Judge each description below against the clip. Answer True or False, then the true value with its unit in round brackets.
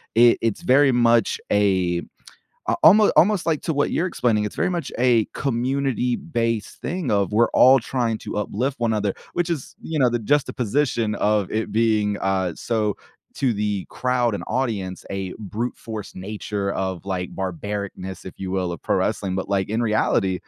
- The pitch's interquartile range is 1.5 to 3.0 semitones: False (4.3 semitones)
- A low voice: True (110 Hz)